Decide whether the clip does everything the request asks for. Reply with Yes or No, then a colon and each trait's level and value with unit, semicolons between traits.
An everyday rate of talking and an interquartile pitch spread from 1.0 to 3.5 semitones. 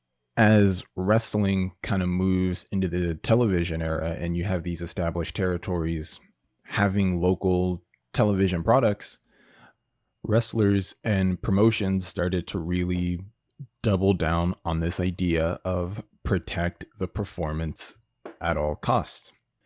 No: slow, 115 wpm; average, 2.9 semitones